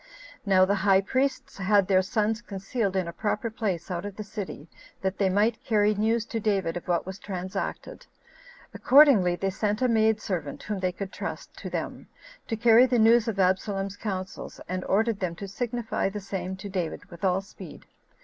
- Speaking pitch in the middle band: No, high, 200 Hz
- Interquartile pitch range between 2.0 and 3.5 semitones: Yes, average, 2.8 semitones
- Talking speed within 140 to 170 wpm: No, average, 190 wpm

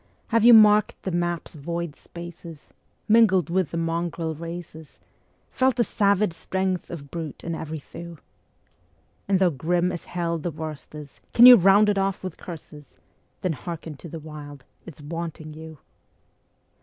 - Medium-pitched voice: Yes, medium, 170 Hz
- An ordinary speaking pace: Yes, average, 155 wpm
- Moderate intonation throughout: Yes, average, 3.0 semitones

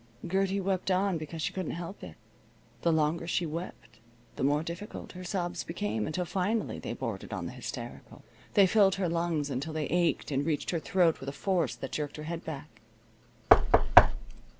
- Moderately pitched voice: Yes, medium, 170 Hz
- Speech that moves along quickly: No, average, 180 wpm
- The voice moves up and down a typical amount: Yes, average, 3.3 semitones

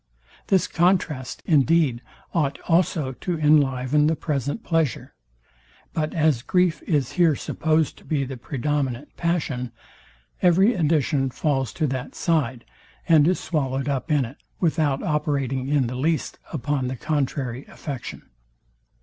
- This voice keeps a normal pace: No, slow, 130 wpm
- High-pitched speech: No, medium, 150 Hz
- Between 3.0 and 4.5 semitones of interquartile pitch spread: Yes, average, 3.5 semitones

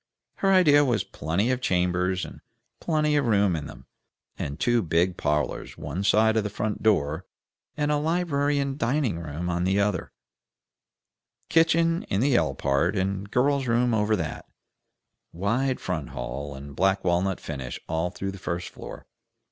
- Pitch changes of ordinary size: No, wide, 7.3 semitones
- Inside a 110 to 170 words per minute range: Yes, average, 165 wpm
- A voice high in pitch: No, low, 100 Hz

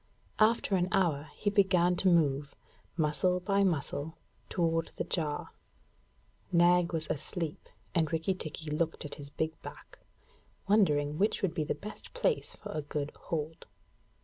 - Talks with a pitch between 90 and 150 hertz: No, medium, 165 Hz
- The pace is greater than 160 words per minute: No, average, 150 wpm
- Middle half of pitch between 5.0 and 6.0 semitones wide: No, average, 3.5 semitones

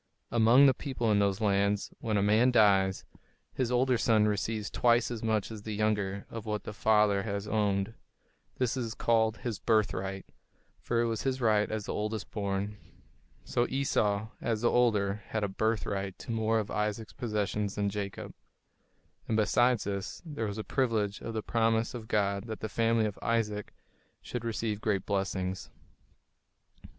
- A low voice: Yes, low, 110 Hz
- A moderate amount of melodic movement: No, narrow, 2.0 semitones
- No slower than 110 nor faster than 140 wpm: No, average, 170 wpm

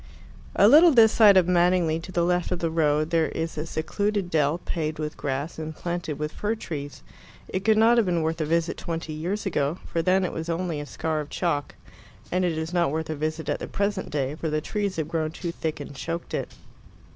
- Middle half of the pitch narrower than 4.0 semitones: Yes, average, 2.8 semitones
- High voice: No, medium, 165 Hz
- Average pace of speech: No, fast, 235 wpm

